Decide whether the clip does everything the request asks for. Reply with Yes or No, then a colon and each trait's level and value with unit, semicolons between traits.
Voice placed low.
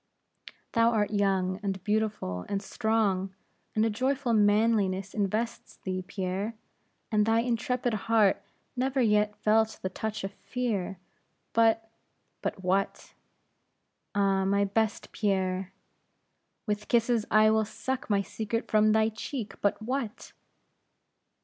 No: high, 215 Hz